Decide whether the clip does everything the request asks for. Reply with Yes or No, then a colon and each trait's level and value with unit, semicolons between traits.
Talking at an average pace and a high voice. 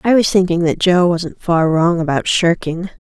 No: average, 195 wpm; medium, 175 Hz